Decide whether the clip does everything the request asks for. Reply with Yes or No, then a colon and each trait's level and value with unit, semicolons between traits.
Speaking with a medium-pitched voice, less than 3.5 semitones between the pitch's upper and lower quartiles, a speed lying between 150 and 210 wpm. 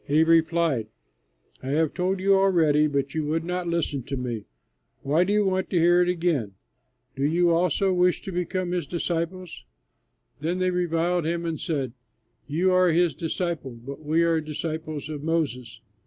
Yes: medium, 165 Hz; average, 3.1 semitones; average, 170 wpm